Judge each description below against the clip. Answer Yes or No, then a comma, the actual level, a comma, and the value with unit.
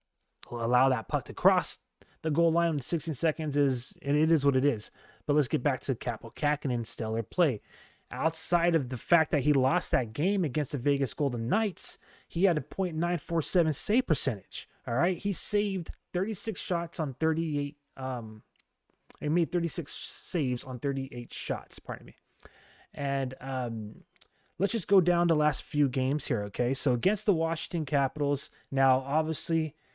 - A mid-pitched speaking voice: Yes, medium, 150 Hz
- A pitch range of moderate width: Yes, average, 4.4 semitones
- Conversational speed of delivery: Yes, average, 170 wpm